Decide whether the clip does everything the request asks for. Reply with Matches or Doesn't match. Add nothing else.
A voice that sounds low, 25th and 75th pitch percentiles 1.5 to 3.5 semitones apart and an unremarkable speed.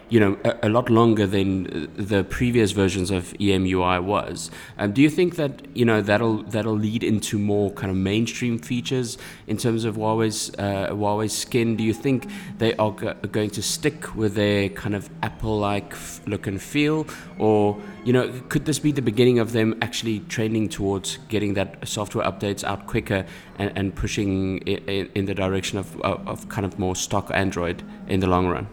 Matches